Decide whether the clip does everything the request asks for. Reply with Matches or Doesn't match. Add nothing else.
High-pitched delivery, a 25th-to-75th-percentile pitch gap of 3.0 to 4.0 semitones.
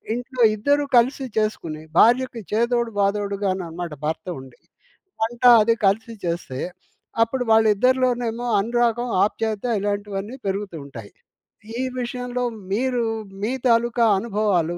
Matches